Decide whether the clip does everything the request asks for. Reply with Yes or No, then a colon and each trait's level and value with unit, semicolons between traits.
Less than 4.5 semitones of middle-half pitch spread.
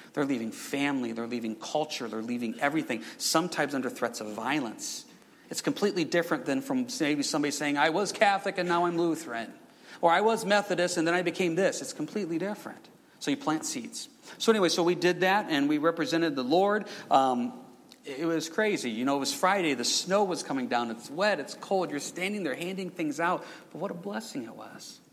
No: average, 5.3 semitones